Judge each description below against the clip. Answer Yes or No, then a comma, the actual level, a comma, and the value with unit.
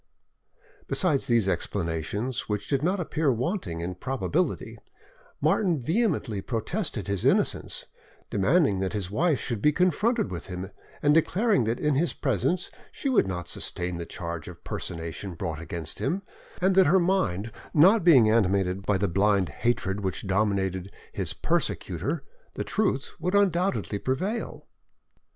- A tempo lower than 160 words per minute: Yes, average, 145 wpm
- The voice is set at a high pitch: No, low, 115 Hz